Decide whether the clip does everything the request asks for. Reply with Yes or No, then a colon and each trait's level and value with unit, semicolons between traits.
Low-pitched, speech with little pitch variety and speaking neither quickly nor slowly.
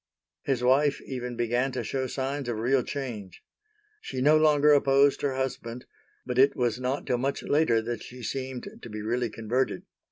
Yes: low, 130 Hz; narrow, 2.3 semitones; average, 180 wpm